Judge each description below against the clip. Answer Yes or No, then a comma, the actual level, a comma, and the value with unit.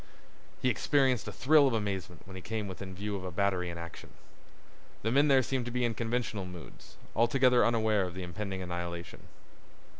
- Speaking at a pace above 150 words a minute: Yes, average, 185 wpm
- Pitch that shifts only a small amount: No, average, 4.9 semitones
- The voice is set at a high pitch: No, low, 105 Hz